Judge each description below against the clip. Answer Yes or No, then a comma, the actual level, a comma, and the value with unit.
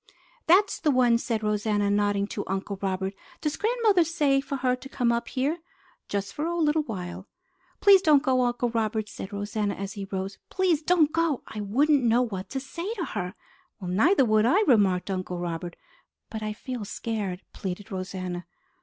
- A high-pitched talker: Yes, high, 225 Hz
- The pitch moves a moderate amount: No, wide, 6.9 semitones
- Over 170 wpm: Yes, average, 180 wpm